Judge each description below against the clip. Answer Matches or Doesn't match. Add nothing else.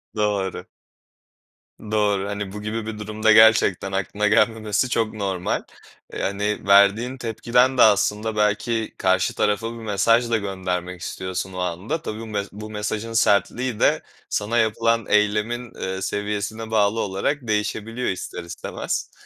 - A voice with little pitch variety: Matches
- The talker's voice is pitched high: Doesn't match